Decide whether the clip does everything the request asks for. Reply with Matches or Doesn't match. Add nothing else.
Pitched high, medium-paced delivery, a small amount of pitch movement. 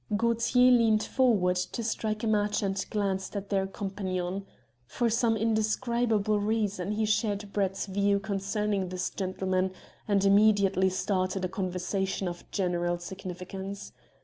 Doesn't match